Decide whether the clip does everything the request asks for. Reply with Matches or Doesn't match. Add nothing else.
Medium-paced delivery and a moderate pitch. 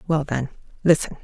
Matches